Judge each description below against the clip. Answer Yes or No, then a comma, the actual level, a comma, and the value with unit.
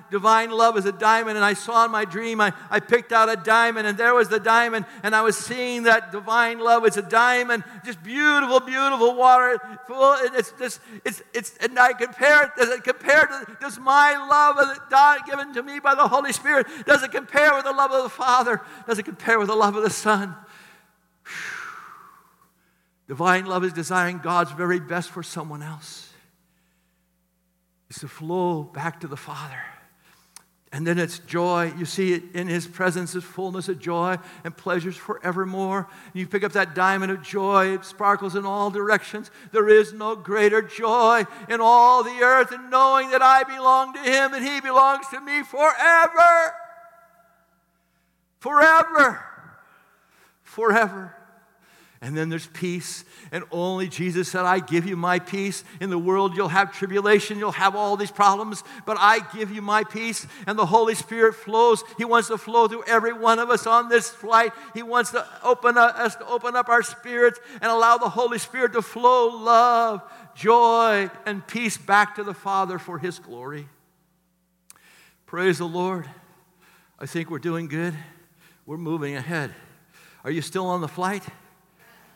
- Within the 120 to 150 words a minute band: No, average, 180 wpm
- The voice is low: No, high, 210 Hz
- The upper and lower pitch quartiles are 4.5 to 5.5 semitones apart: Yes, average, 4.8 semitones